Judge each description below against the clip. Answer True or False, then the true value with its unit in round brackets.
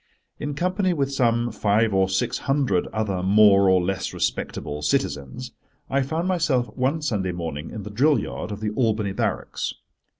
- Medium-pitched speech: False (110 Hz)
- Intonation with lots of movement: True (6.2 semitones)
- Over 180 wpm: False (165 wpm)